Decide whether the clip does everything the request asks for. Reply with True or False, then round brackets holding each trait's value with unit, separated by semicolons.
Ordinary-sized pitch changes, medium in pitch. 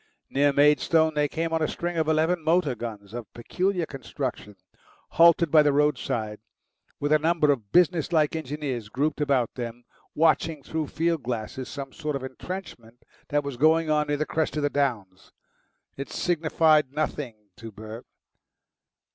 True (4.4 semitones; 145 Hz)